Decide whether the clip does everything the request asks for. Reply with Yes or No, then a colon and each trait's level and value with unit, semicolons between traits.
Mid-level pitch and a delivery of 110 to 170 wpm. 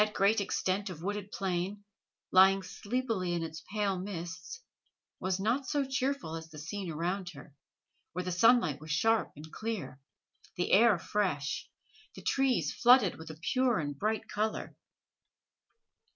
No: high, 195 Hz; average, 150 wpm